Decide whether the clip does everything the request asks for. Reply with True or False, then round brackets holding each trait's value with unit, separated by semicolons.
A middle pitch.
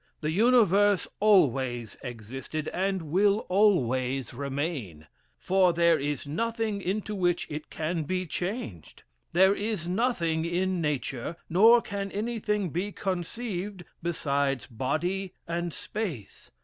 True (175 Hz)